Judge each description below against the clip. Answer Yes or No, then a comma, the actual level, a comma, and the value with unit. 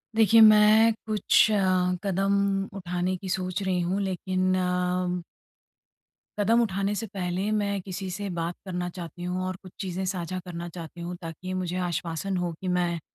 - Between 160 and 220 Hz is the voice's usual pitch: Yes, medium, 185 Hz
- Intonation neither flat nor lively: No, narrow, 1.8 semitones